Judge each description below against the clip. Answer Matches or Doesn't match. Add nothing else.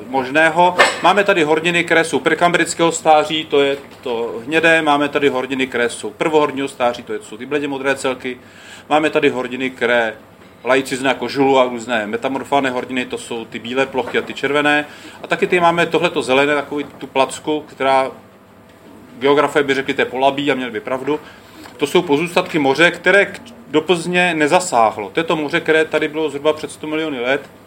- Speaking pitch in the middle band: Matches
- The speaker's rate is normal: Doesn't match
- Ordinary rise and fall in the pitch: Matches